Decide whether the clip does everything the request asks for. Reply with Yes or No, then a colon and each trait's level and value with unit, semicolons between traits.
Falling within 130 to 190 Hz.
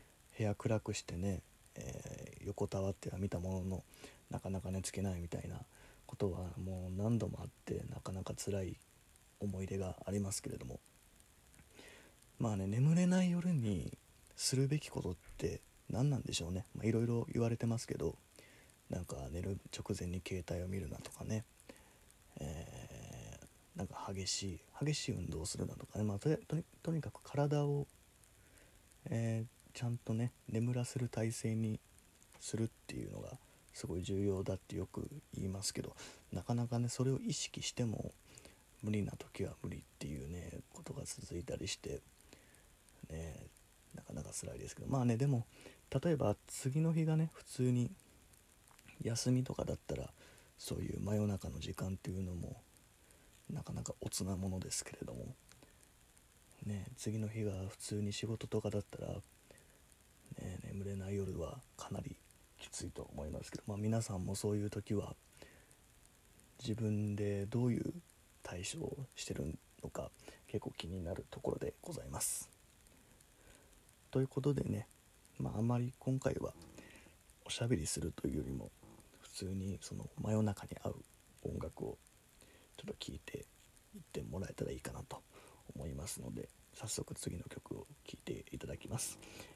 No: low, 105 Hz